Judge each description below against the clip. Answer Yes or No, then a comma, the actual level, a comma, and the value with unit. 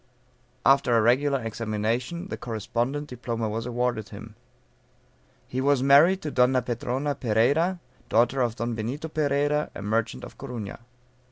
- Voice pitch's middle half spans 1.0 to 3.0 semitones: No, average, 3.6 semitones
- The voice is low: Yes, low, 125 Hz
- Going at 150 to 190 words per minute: No, average, 140 wpm